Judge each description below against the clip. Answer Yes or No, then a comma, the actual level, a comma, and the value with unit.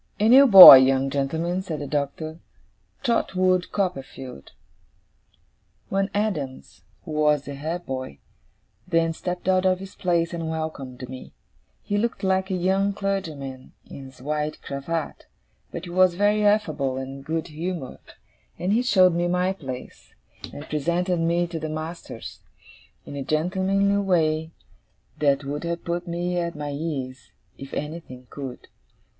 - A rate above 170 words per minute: No, average, 145 wpm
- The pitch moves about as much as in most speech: Yes, average, 4.6 semitones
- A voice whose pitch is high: No, medium, 165 Hz